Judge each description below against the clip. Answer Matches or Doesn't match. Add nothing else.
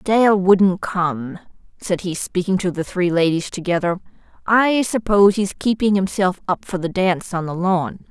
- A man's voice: Doesn't match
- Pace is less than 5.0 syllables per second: Matches